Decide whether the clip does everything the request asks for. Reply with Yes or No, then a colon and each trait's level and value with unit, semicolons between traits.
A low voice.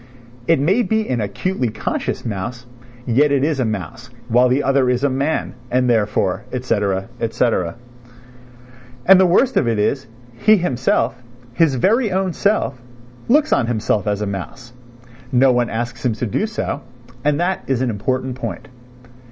Yes: low, 125 Hz